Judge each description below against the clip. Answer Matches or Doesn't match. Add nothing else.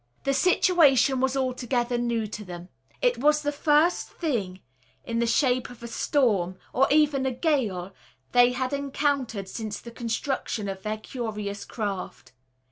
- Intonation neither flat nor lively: Matches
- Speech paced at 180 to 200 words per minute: Doesn't match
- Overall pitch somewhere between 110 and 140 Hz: Doesn't match